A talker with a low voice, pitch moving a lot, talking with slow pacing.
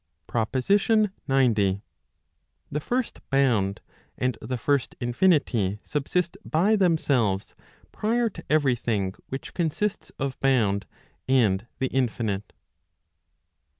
Yes: low, 130 Hz; wide, 6.6 semitones; slow, 100 wpm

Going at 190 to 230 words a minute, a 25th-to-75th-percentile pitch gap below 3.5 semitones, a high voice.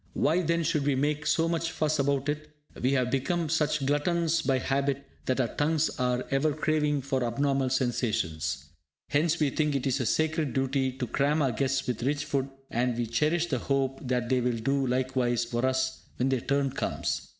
No: average, 195 wpm; average, 2.9 semitones; low, 135 Hz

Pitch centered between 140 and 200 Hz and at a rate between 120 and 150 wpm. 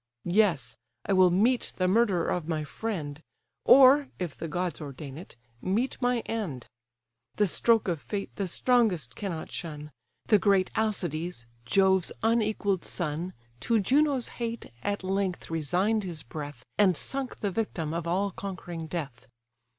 Yes: medium, 185 Hz; average, 145 wpm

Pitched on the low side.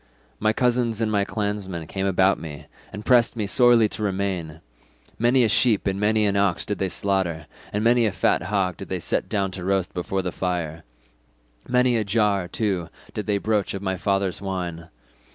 Yes: low, 100 Hz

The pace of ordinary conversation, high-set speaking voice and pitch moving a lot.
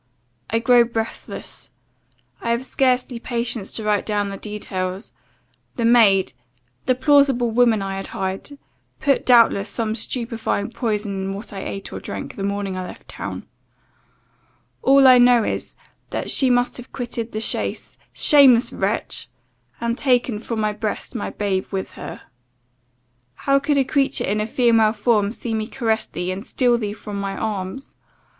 No: average, 160 wpm; high, 225 Hz; average, 3.3 semitones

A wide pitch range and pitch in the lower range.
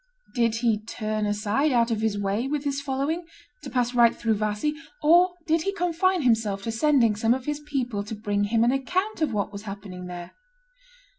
No: wide, 5.8 semitones; high, 235 Hz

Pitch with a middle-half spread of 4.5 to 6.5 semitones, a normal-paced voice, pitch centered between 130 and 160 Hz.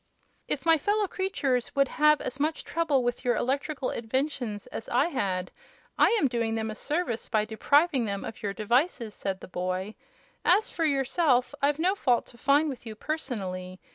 No: wide, 5.5 semitones; average, 180 wpm; very high, 255 Hz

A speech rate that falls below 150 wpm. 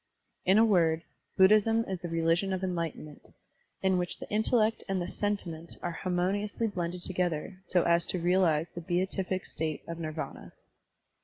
No: average, 155 wpm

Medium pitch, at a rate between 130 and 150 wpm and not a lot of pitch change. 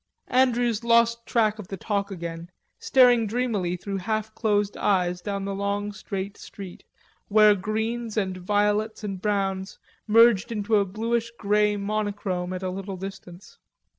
No: high, 205 Hz; average, 145 wpm; narrow, 2.3 semitones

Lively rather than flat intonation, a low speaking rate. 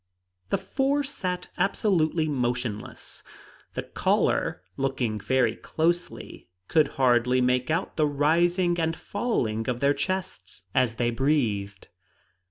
Yes: wide, 6.2 semitones; slow, 115 wpm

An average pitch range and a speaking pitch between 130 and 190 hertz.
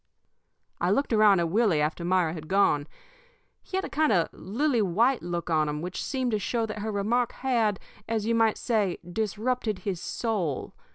No: average, 4.9 semitones; high, 210 Hz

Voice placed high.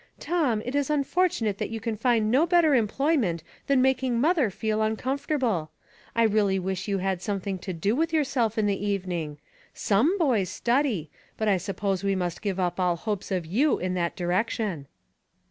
Yes: high, 215 Hz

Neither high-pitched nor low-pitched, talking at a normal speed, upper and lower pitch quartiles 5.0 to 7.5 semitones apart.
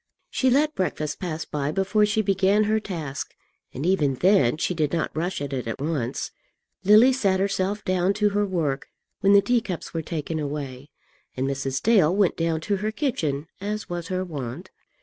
Yes: medium, 180 Hz; average, 185 wpm; wide, 5.5 semitones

